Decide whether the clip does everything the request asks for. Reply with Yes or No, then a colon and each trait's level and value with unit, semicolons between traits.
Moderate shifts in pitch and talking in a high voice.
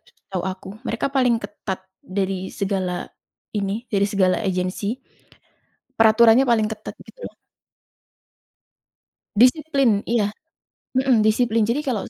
Yes: average, 3.7 semitones; high, 215 Hz